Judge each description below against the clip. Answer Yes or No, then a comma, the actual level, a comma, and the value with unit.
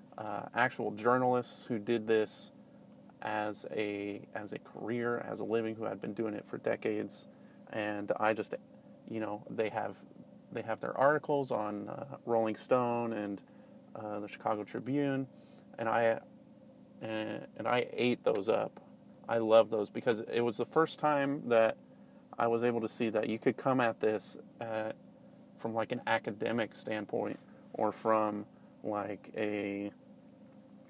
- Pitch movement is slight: Yes, narrow, 2.1 semitones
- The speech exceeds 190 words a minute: No, average, 155 wpm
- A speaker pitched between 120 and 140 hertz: No, low, 110 Hz